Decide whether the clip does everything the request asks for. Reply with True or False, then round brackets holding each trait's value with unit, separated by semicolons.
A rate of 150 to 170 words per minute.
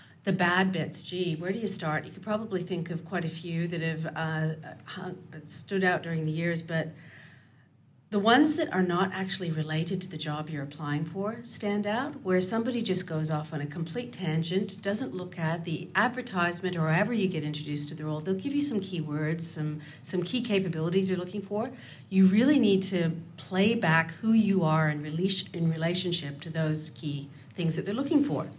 False (200 wpm)